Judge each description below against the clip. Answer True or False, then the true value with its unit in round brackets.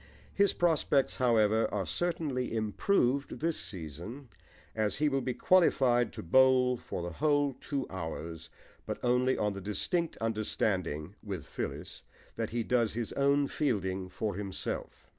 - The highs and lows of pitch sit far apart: True (5.8 semitones)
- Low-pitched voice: True (120 Hz)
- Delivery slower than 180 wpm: True (140 wpm)